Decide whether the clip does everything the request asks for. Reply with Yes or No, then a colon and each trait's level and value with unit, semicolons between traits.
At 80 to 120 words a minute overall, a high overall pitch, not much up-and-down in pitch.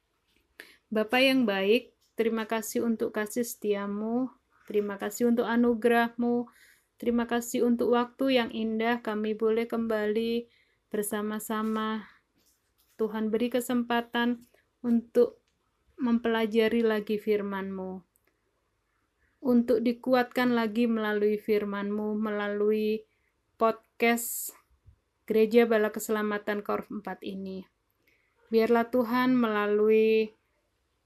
Yes: slow, 85 wpm; high, 225 Hz; narrow, 2.0 semitones